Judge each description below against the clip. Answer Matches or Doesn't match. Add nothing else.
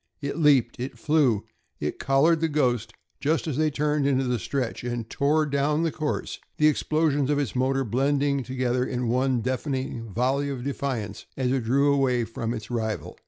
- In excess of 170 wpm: Matches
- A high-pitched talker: Doesn't match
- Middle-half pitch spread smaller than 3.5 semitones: Matches